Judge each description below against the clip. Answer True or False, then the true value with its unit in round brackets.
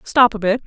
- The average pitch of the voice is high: True (225 Hz)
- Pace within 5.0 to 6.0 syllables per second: True (5.6 syllables/s)